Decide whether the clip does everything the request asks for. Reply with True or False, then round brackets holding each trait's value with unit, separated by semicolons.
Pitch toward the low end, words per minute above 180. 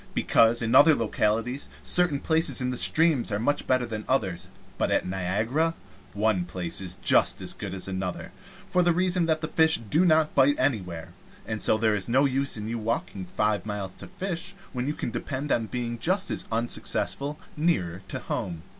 True (120 Hz; 190 wpm)